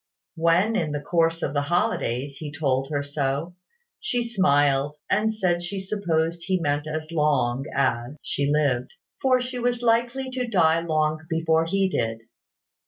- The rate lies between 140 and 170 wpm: Yes, average, 160 wpm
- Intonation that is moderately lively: Yes, average, 5.0 semitones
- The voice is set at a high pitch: No, medium, 160 Hz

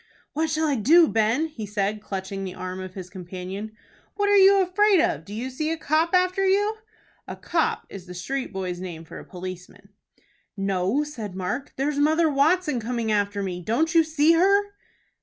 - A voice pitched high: Yes, very high, 250 Hz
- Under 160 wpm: No, average, 190 wpm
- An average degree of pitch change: No, wide, 9.0 semitones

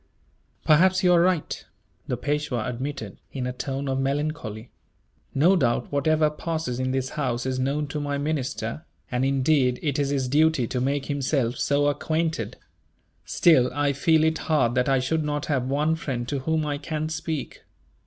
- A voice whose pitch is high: No, medium, 145 Hz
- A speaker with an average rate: Yes, average, 175 wpm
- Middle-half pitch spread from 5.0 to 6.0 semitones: No, average, 3.2 semitones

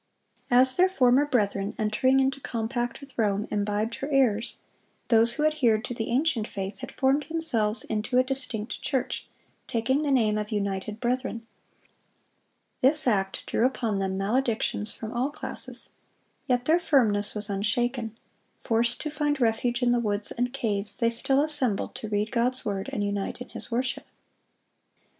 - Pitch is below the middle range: No, high, 235 Hz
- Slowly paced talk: No, average, 160 wpm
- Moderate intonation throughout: Yes, average, 3.8 semitones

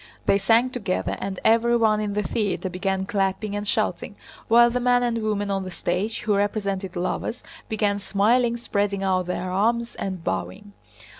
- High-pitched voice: Yes, high, 205 Hz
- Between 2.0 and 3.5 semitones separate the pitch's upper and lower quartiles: Yes, average, 3.0 semitones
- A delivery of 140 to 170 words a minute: Yes, average, 155 wpm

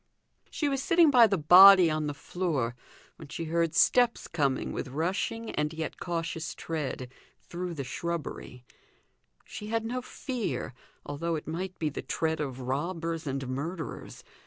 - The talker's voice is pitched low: No, medium, 165 Hz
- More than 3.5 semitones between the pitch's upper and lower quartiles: Yes, average, 4.2 semitones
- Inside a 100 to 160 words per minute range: Yes, average, 155 wpm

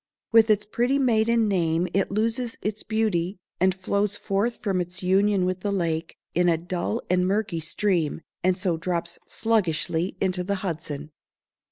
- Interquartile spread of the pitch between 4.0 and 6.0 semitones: No, average, 3.5 semitones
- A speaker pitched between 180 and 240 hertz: Yes, high, 190 Hz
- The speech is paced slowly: No, average, 160 wpm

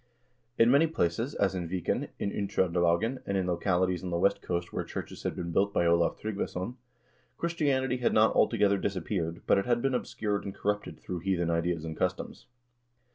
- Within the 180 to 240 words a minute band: Yes, average, 190 wpm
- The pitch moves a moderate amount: Yes, average, 4.2 semitones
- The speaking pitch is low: Yes, very low, 95 Hz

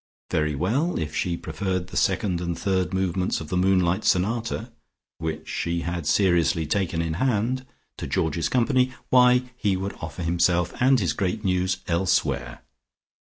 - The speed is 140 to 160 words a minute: Yes, average, 155 wpm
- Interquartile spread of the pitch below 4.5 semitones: Yes, average, 3.8 semitones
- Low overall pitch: Yes, very low, 90 Hz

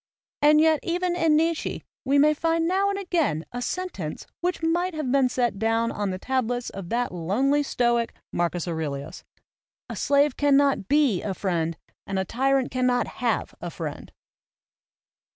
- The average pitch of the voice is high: Yes, very high, 260 Hz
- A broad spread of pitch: Yes, wide, 7.6 semitones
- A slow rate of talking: No, average, 160 wpm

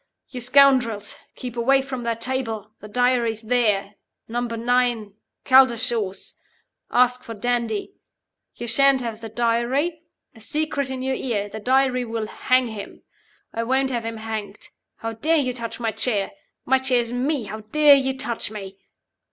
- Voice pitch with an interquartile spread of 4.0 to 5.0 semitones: No, average, 2.7 semitones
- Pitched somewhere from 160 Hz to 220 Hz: No, high, 240 Hz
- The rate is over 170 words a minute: No, average, 160 wpm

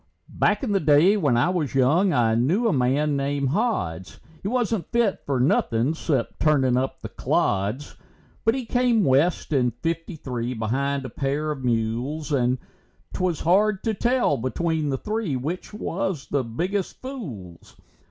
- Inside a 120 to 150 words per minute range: No, average, 160 wpm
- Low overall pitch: No, medium, 145 Hz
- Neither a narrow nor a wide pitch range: No, wide, 7.0 semitones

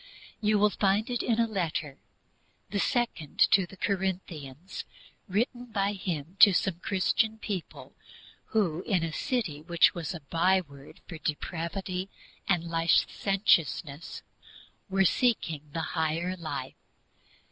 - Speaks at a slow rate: Yes, slow, 125 wpm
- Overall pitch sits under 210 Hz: Yes, medium, 185 Hz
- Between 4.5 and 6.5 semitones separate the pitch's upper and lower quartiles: No, average, 3.7 semitones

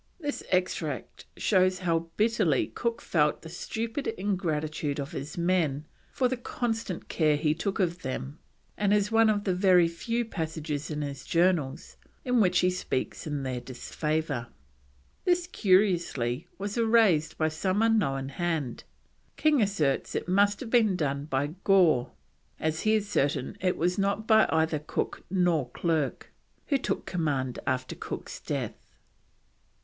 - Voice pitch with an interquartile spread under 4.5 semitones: No, wide, 5.4 semitones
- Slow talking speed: No, average, 150 wpm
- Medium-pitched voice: Yes, medium, 175 Hz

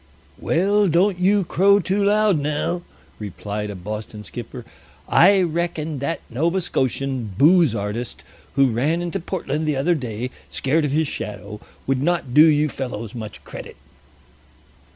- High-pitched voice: No, medium, 150 Hz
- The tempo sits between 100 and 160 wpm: Yes, average, 150 wpm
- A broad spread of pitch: Yes, wide, 6.5 semitones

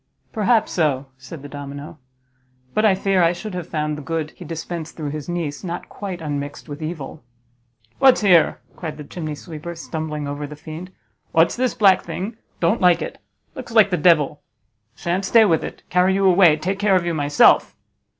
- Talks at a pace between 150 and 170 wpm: No, average, 190 wpm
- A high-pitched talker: No, medium, 170 Hz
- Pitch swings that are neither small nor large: Yes, average, 3.8 semitones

